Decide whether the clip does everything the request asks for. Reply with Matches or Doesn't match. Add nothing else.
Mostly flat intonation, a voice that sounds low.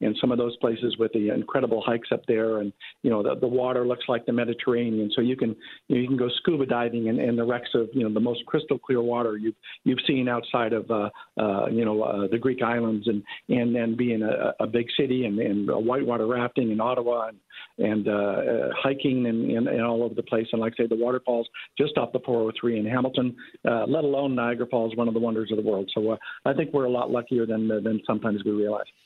Matches